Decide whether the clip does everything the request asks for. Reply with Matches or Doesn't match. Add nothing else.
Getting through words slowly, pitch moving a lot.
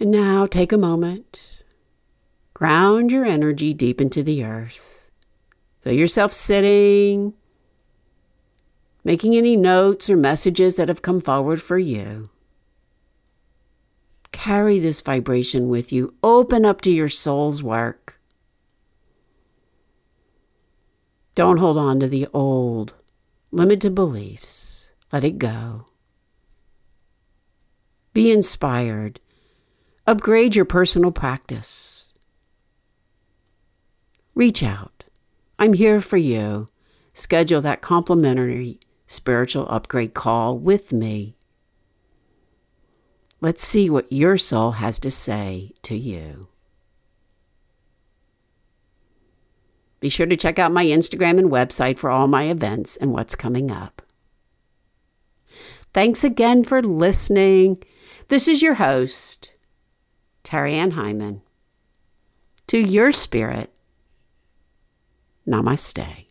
Matches